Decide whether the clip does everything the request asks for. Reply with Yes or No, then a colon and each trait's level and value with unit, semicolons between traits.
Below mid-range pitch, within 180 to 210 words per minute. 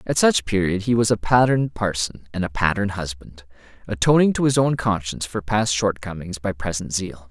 Yes: low, 100 Hz; average, 190 wpm